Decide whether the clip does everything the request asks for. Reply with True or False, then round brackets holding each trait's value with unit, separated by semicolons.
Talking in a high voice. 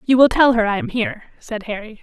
True (230 Hz)